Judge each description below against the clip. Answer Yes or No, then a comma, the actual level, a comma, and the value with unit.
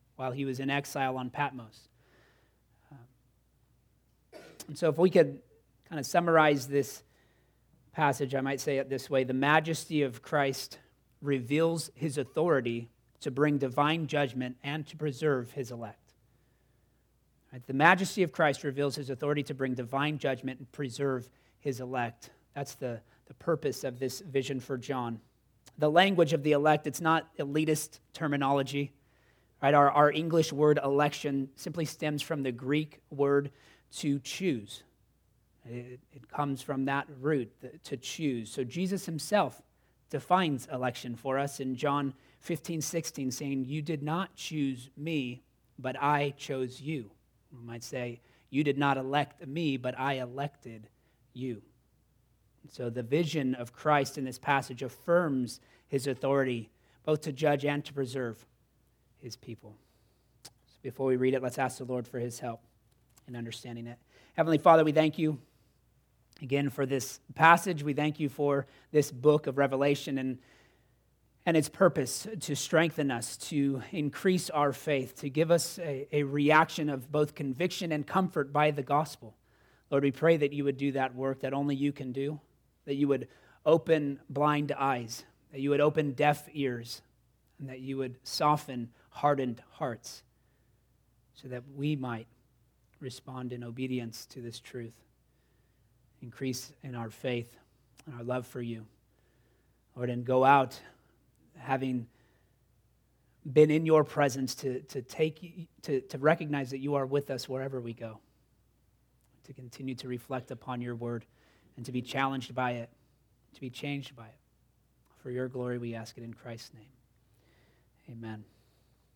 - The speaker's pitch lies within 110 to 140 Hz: Yes, low, 135 Hz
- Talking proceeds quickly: No, average, 155 wpm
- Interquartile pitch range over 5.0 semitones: No, average, 3.1 semitones